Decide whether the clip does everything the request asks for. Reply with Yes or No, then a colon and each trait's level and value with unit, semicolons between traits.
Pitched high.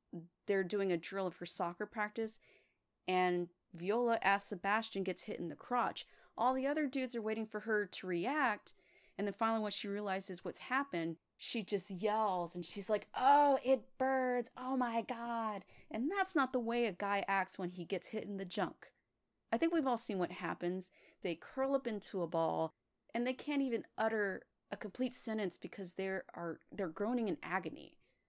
Yes: high, 210 Hz